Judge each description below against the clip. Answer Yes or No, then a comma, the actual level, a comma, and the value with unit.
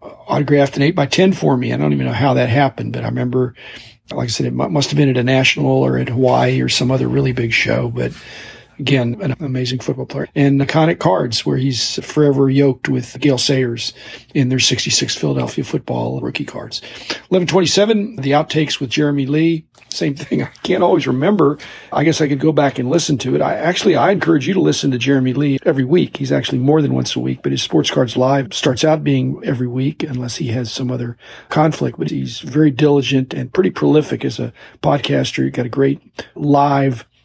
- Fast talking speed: Yes, fast, 210 wpm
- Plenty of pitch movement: No, average, 2.9 semitones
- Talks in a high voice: No, low, 135 Hz